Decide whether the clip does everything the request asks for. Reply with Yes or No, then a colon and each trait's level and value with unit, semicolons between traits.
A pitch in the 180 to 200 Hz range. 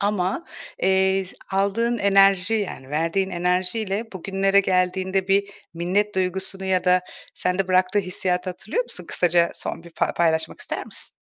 Yes: high, 190 Hz